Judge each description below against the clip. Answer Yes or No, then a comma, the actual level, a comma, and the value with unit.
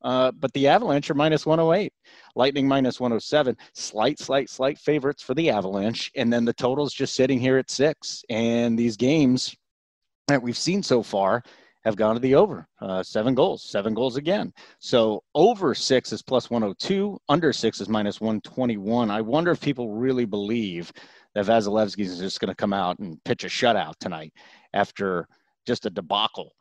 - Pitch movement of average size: Yes, average, 3.9 semitones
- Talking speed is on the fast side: No, average, 180 wpm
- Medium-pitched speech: No, low, 120 Hz